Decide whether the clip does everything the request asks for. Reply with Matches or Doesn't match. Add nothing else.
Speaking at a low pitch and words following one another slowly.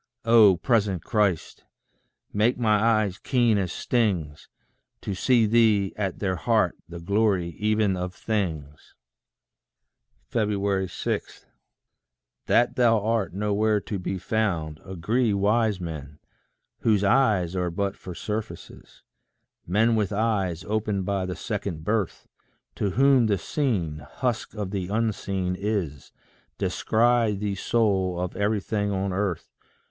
Matches